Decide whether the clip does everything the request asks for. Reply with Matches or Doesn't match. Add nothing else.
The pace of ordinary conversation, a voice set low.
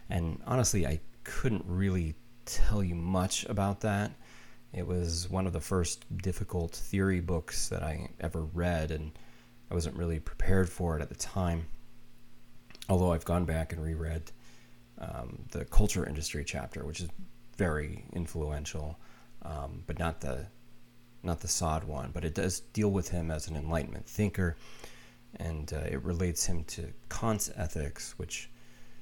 Matches